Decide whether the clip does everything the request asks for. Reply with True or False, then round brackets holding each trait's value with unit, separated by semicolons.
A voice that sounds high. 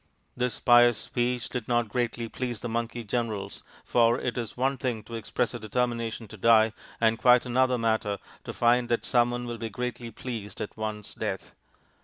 False (120 Hz)